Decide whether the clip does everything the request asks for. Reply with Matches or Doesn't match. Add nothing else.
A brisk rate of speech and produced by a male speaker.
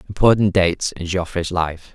Doesn't match